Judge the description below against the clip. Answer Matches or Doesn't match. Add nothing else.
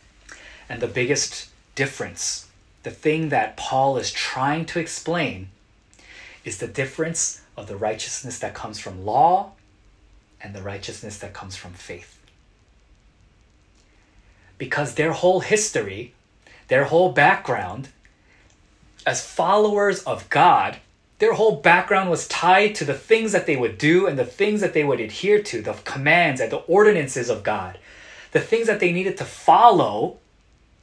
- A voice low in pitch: Doesn't match